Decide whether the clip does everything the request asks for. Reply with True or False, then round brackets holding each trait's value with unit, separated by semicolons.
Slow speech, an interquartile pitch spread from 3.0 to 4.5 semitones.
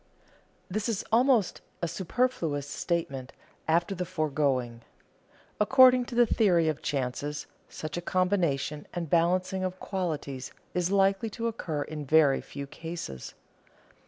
False (130 wpm; 5.0 semitones)